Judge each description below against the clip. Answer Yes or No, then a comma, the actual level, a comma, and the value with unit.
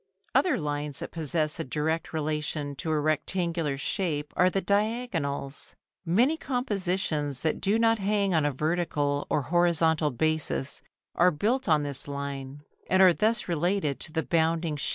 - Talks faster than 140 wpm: Yes, average, 155 wpm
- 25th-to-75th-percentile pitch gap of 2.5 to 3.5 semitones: No, average, 4.2 semitones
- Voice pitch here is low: No, medium, 160 Hz